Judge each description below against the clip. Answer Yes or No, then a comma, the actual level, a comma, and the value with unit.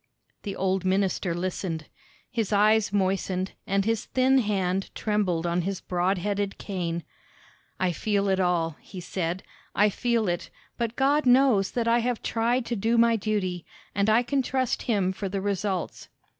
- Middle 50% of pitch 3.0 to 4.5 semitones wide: Yes, average, 3.5 semitones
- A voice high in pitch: Yes, high, 200 Hz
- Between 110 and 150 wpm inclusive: No, average, 165 wpm